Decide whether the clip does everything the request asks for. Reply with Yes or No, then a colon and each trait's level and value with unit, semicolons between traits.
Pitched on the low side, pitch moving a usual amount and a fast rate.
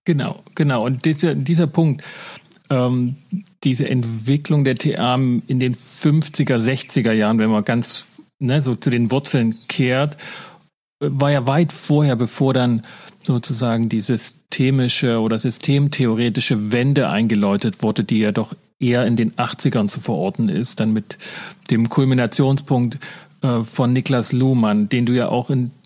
No: low, 130 Hz; average, 3.5 semitones; average, 145 wpm